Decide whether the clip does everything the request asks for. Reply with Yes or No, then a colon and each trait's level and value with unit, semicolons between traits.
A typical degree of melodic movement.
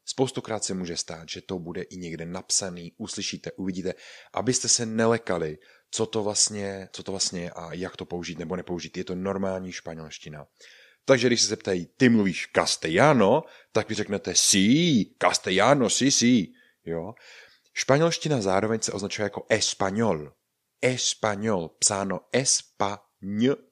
Yes: average, 4.1 semitones